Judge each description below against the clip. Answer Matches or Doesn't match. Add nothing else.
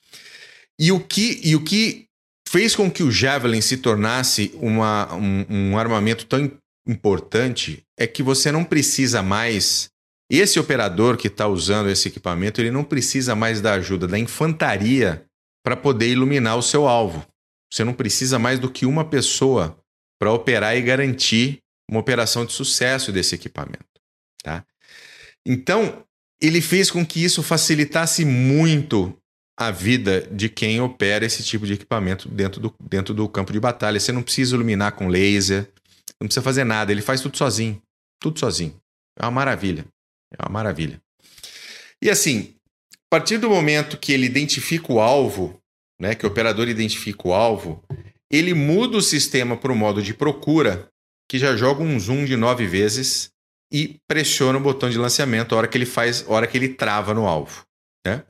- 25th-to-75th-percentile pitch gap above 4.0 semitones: Matches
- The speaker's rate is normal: Matches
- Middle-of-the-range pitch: Doesn't match